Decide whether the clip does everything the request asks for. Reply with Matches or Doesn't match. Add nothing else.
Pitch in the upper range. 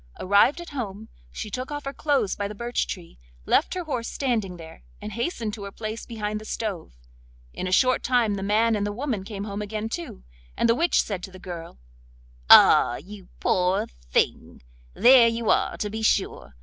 Matches